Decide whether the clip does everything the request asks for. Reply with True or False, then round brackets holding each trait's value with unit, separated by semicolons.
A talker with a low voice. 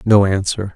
True (100 Hz)